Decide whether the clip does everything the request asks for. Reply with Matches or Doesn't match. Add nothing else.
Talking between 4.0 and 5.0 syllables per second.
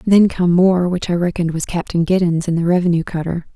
Doesn't match